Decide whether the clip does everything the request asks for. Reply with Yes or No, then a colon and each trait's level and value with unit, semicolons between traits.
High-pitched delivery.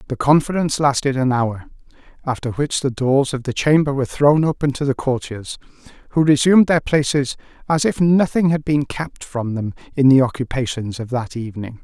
No: low, 135 Hz